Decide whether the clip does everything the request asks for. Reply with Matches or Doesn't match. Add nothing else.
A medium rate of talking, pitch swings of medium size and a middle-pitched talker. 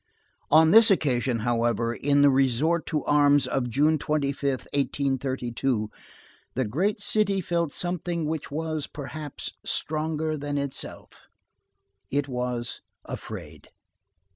Doesn't match